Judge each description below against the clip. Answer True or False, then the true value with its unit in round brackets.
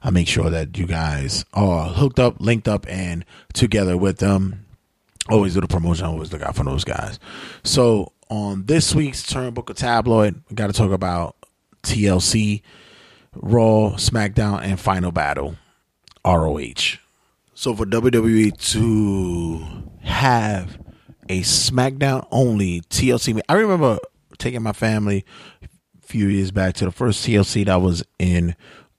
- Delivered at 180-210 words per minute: False (145 wpm)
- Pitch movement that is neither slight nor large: True (4.1 semitones)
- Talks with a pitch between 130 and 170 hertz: False (100 Hz)